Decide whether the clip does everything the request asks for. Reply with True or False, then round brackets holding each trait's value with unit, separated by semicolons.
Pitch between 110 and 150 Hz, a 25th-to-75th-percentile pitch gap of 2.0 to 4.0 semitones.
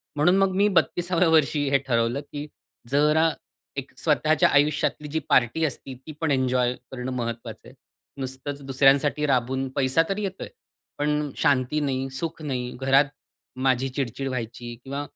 True (140 Hz; 2.6 semitones)